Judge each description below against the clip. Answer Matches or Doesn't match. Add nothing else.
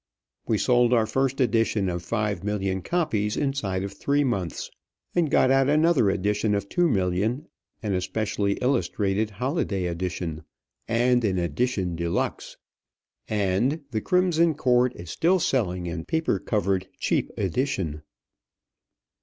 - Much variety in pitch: Matches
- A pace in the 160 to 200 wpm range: Doesn't match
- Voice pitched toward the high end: Doesn't match